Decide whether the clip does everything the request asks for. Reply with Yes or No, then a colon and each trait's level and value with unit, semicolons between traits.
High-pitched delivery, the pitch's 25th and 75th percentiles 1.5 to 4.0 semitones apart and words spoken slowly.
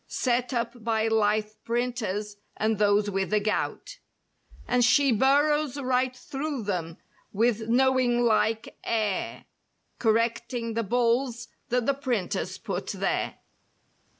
Yes: high, 235 Hz; average, 2.7 semitones; slow, 120 wpm